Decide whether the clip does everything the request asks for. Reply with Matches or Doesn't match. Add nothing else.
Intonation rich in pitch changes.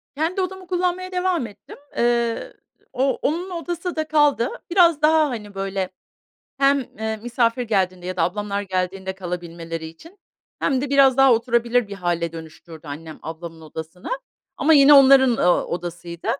Matches